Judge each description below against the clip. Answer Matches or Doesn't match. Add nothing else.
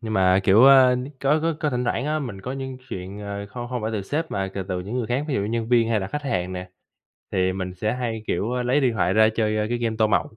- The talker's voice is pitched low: Matches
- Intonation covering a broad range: Doesn't match